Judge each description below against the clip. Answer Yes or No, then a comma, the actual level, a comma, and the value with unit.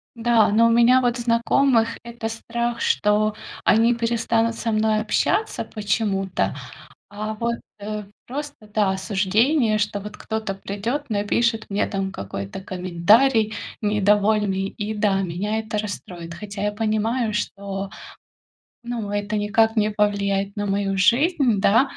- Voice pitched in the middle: No, high, 215 Hz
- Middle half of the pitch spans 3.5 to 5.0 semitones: No, narrow, 2.4 semitones